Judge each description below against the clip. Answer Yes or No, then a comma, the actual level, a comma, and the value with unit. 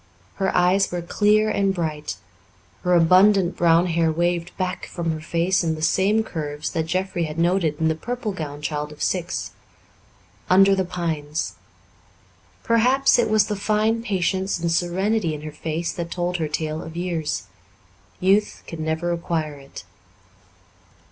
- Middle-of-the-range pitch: Yes, medium, 175 Hz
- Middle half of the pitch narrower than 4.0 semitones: Yes, average, 3.3 semitones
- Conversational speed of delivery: Yes, average, 155 wpm